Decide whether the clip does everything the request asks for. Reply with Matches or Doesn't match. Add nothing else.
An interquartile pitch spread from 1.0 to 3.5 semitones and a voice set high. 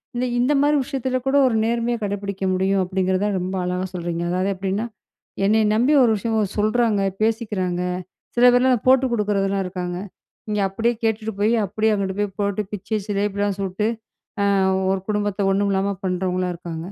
Matches